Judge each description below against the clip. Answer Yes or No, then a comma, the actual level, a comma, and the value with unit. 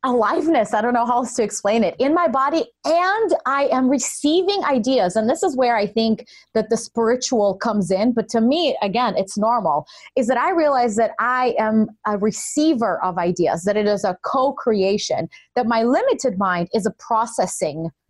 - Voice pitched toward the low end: No, high, 235 Hz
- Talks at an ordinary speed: Yes, average, 190 wpm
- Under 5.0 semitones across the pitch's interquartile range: Yes, average, 4.1 semitones